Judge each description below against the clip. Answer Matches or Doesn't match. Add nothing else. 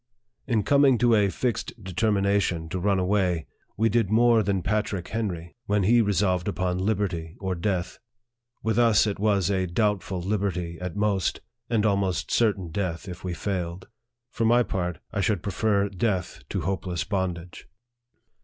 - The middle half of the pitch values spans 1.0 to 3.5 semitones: Matches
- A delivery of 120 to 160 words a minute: Doesn't match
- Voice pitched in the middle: Doesn't match